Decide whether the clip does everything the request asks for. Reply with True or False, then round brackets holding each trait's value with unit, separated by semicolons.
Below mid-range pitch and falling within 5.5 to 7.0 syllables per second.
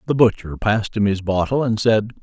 True (110 Hz; 5.6 syllables/s)